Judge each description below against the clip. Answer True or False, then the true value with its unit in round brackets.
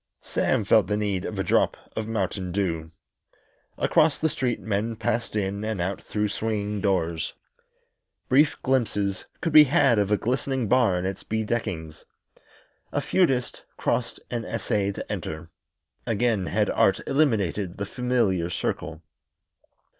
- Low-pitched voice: True (105 Hz)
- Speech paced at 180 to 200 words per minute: False (140 wpm)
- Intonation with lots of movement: False (4.0 semitones)